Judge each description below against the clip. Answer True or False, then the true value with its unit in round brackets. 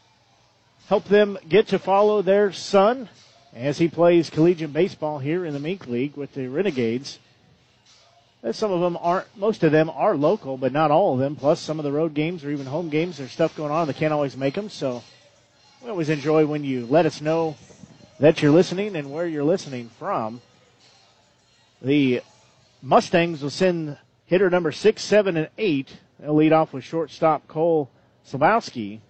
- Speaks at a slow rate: False (180 wpm)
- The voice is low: False (155 Hz)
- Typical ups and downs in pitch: True (4.2 semitones)